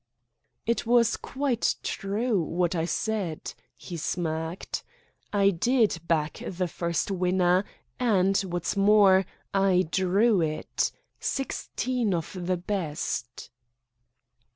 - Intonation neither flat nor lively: Yes, average, 3.7 semitones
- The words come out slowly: Yes, slow, 105 wpm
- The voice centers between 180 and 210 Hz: Yes, high, 190 Hz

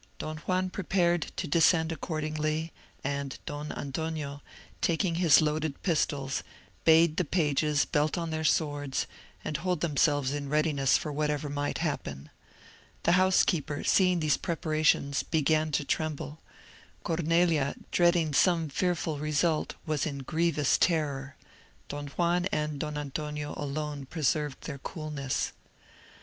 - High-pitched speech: No, medium, 155 Hz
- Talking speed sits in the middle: No, slow, 120 wpm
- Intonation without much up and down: Yes, narrow, 2.3 semitones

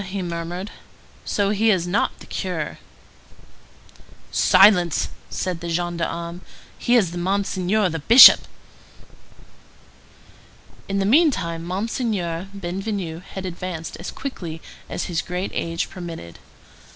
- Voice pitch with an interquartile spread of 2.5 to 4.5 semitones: Yes, average, 2.8 semitones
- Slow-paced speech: Yes, slow, 110 wpm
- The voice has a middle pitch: Yes, medium, 180 Hz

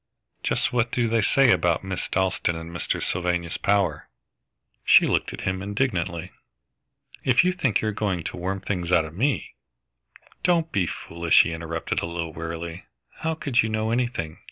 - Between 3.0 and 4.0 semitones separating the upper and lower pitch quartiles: No, wide, 5.4 semitones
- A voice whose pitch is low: Yes, very low, 95 Hz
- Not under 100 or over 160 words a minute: No, average, 175 wpm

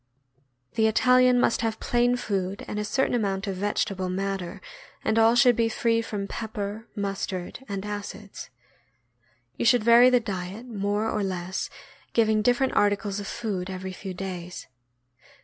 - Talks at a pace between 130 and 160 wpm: Yes, average, 150 wpm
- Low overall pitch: No, high, 210 Hz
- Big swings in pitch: No, average, 2.9 semitones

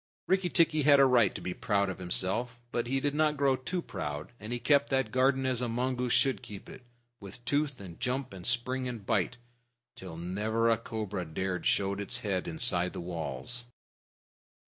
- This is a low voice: Yes, low, 120 Hz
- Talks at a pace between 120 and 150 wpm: No, average, 190 wpm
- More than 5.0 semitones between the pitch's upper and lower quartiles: Yes, wide, 5.4 semitones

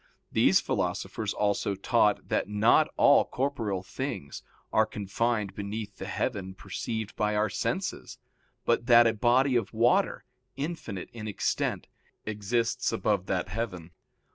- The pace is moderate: No, slow, 130 wpm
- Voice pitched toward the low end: Yes, low, 110 Hz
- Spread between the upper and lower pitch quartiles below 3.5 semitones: Yes, average, 2.9 semitones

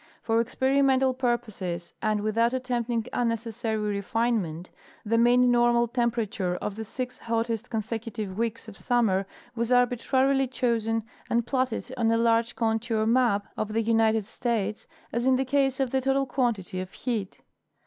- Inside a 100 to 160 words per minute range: Yes, average, 150 wpm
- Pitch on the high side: Yes, high, 230 Hz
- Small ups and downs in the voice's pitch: Yes, narrow, 2.2 semitones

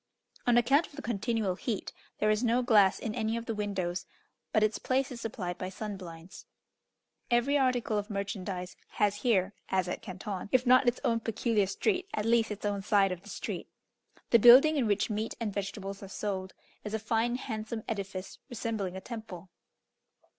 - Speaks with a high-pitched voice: Yes, high, 215 Hz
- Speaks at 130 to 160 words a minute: No, average, 185 wpm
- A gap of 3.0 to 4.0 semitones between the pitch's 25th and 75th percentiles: Yes, average, 3.3 semitones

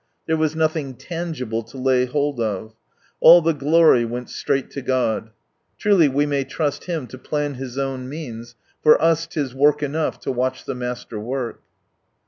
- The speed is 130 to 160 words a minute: No, average, 170 wpm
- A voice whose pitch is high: No, low, 135 Hz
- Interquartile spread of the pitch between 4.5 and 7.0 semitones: No, average, 3.8 semitones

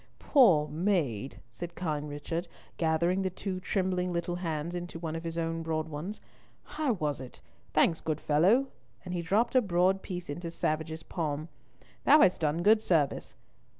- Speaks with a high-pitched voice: No, medium, 170 Hz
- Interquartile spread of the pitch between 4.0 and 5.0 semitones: No, average, 2.9 semitones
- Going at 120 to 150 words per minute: No, average, 165 wpm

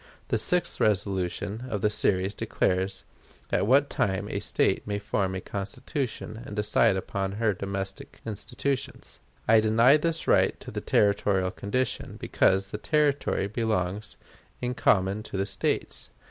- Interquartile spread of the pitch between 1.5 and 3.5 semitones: Yes, average, 3.0 semitones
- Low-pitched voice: Yes, low, 105 Hz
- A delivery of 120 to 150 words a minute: Yes, average, 145 wpm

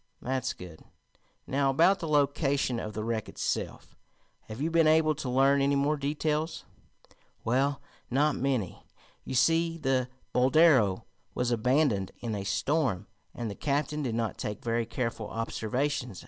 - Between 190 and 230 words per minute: No, average, 145 wpm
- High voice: No, low, 135 Hz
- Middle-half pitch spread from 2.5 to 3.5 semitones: No, average, 4.4 semitones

